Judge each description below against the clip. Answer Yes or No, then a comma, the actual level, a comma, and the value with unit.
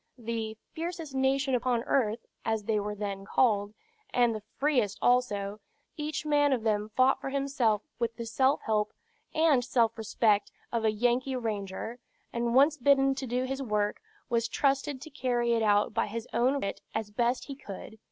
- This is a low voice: No, high, 240 Hz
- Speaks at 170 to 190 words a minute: Yes, average, 175 wpm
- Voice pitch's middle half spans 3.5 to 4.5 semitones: Yes, average, 3.8 semitones